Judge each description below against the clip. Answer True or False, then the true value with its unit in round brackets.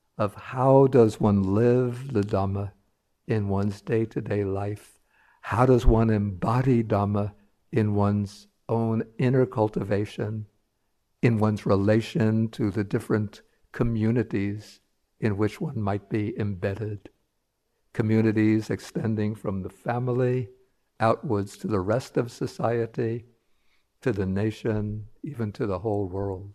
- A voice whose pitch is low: True (110 Hz)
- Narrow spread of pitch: True (2.1 semitones)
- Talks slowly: True (120 wpm)